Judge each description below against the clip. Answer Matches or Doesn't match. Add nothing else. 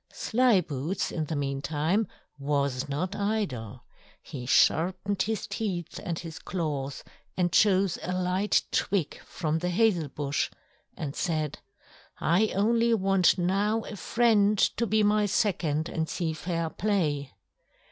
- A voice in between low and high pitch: Matches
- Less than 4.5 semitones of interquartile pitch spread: Doesn't match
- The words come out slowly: Matches